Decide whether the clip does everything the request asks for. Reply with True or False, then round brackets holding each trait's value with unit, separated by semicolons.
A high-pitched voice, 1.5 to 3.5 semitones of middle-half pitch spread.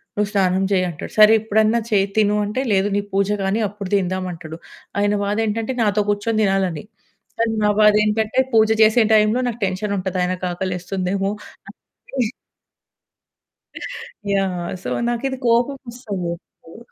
True (205 Hz; 2.5 semitones)